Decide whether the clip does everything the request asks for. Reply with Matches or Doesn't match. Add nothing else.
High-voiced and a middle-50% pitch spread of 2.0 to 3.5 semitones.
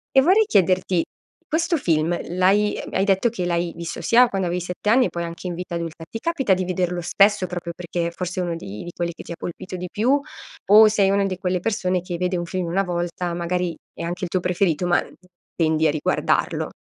Doesn't match